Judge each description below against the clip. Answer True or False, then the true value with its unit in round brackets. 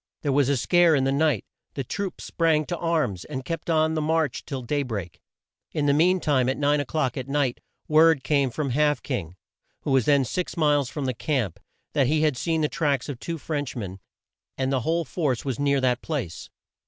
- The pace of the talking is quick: True (215 wpm)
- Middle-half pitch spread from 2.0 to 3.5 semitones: True (3.2 semitones)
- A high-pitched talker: False (145 Hz)